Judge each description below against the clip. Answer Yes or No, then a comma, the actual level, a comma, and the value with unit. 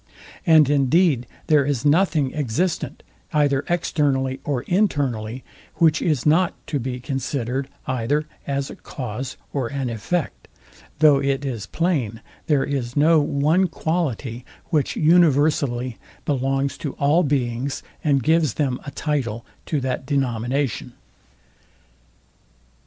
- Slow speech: Yes, slow, 120 wpm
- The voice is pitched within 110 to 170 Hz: Yes, medium, 140 Hz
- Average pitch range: Yes, average, 3.1 semitones